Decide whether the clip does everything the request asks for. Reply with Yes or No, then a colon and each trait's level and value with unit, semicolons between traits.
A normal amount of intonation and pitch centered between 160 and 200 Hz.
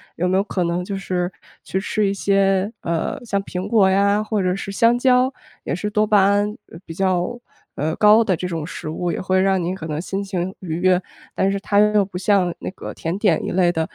No: narrow, 2.3 semitones; high, 190 Hz